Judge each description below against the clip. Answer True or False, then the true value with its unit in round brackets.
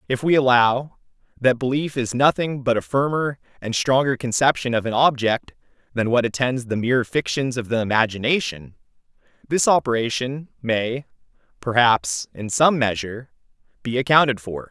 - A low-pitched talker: True (125 Hz)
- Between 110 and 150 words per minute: True (145 wpm)